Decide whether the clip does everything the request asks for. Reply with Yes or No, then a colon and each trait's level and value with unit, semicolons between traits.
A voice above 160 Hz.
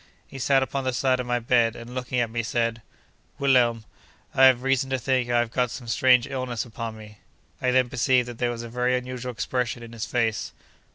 No: low, 125 Hz